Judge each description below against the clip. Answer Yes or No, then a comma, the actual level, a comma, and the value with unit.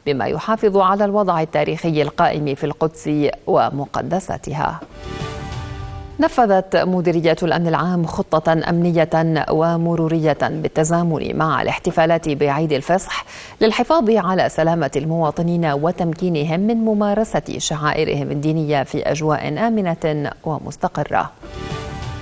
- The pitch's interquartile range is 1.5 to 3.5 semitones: Yes, average, 3.0 semitones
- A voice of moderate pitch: Yes, medium, 165 Hz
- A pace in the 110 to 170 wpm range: No, average, 90 wpm